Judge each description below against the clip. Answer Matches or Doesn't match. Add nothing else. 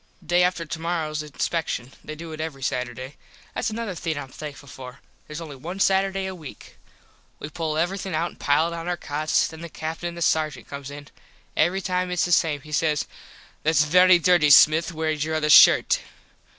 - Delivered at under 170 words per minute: Doesn't match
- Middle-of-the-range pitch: Matches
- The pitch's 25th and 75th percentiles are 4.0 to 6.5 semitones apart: Doesn't match